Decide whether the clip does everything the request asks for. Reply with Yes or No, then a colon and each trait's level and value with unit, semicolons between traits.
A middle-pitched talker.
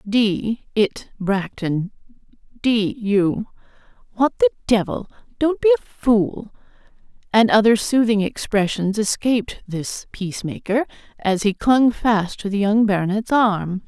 No: high, 215 Hz